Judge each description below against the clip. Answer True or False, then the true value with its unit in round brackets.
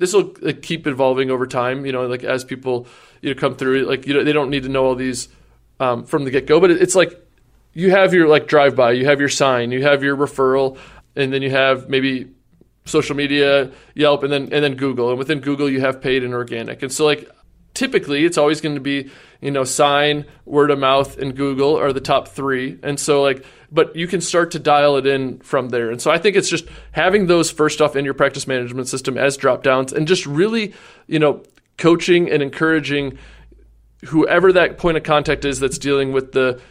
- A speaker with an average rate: False (225 wpm)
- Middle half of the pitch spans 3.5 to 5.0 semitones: False (2.4 semitones)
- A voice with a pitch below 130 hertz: False (140 Hz)